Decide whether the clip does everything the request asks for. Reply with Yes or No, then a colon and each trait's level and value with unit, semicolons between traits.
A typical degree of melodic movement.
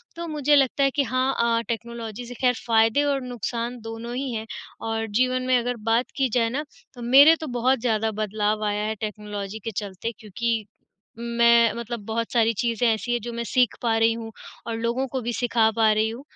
No: narrow, 2.1 semitones